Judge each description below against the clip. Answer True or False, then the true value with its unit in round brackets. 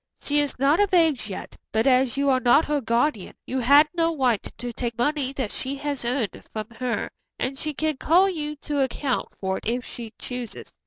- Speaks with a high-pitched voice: True (265 Hz)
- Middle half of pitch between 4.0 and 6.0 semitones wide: False (3.6 semitones)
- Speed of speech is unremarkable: False (210 wpm)